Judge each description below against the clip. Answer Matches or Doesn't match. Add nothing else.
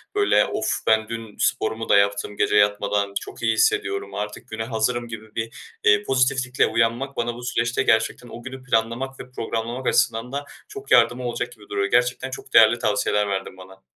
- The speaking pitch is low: Matches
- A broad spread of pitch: Doesn't match